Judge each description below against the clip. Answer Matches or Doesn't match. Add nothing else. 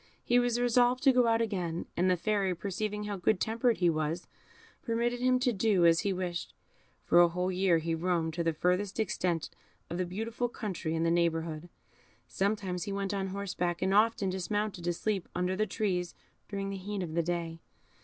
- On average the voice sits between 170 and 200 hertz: Matches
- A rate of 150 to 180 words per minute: Doesn't match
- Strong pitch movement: Doesn't match